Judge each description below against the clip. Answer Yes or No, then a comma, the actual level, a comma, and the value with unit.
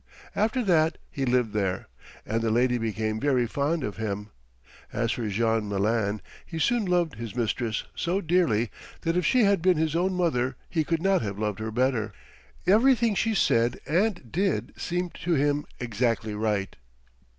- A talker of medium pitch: No, low, 125 Hz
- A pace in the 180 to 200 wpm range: No, average, 170 wpm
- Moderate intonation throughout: No, wide, 8.1 semitones